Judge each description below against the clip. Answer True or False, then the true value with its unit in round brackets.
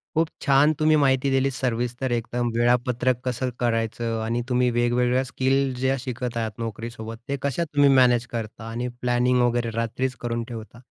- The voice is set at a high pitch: False (125 Hz)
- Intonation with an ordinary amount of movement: False (2.1 semitones)